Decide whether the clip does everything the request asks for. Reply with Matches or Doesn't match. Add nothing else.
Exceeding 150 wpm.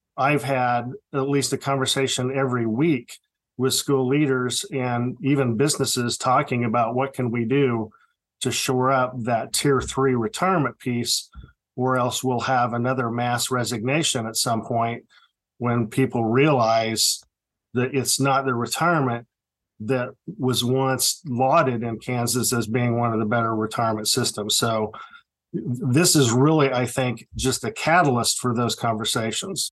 Doesn't match